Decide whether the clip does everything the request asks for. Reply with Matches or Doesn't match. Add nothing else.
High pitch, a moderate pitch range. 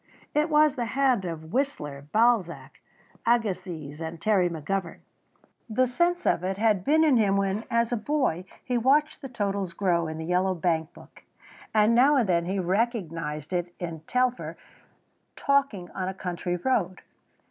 Doesn't match